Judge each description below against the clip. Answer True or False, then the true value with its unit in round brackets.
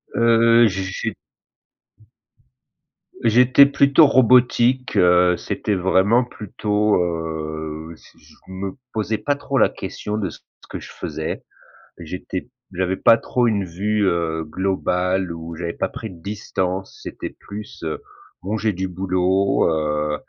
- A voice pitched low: True (95 Hz)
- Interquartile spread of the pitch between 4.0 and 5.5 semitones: True (4.3 semitones)